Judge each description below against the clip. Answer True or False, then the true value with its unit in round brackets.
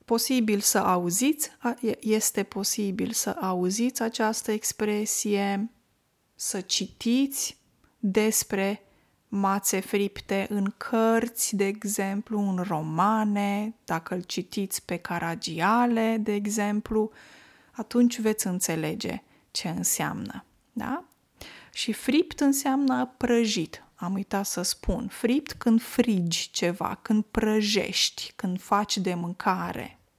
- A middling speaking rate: False (100 wpm)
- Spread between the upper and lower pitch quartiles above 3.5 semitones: False (2.9 semitones)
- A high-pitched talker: True (210 Hz)